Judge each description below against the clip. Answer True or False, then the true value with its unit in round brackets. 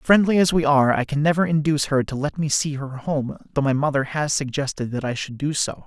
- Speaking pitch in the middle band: True (145 Hz)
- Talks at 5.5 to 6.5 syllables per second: True (5.9 syllables/s)